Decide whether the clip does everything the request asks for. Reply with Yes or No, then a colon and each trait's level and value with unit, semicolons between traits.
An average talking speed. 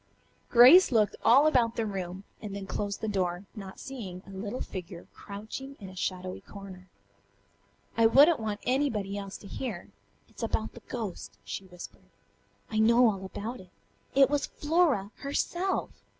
Yes: average, 160 wpm